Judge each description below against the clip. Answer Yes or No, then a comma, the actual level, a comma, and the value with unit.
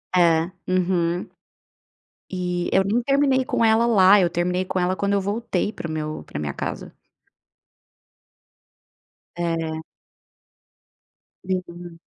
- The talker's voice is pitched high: No, medium, 180 Hz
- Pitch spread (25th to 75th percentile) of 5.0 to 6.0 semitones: No, average, 2.9 semitones